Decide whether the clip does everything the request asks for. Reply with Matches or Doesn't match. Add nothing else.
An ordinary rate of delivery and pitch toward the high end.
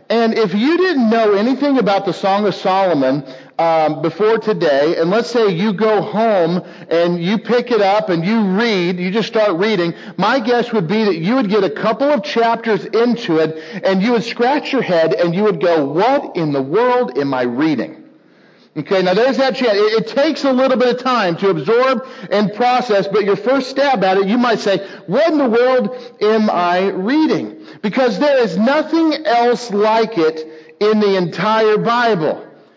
Matches